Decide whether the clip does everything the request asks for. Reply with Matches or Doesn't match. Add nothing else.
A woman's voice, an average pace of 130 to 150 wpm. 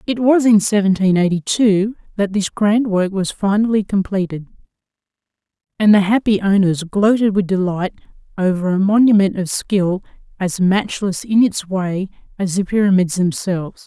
Matches